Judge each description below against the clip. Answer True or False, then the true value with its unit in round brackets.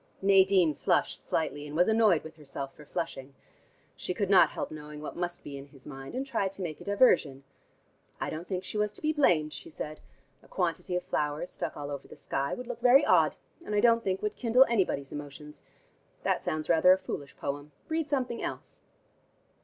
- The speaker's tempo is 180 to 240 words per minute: True (205 wpm)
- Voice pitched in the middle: True (175 Hz)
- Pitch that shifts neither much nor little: False (6.1 semitones)